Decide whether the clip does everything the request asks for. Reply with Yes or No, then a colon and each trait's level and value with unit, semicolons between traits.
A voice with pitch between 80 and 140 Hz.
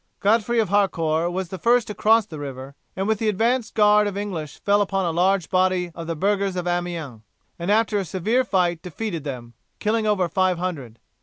No: high, 190 Hz